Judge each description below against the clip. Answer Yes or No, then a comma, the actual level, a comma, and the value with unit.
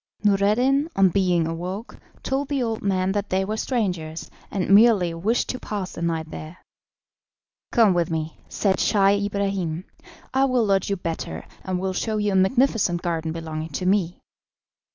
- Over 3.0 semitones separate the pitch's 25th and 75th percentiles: Yes, average, 3.8 semitones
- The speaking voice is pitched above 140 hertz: Yes, high, 190 Hz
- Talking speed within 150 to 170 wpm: Yes, average, 165 wpm